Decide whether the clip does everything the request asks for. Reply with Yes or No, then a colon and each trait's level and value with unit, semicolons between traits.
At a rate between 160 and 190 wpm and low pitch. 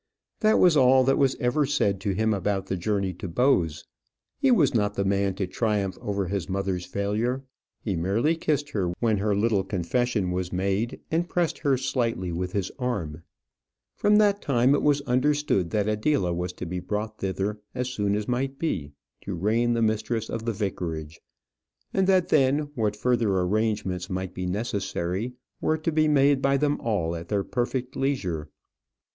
Yes: average, 180 wpm; low, 105 Hz